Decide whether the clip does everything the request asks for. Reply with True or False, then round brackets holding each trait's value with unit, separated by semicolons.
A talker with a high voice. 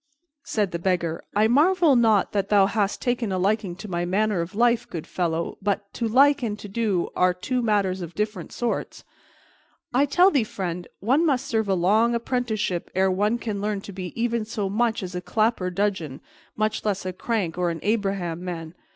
True (205 Hz)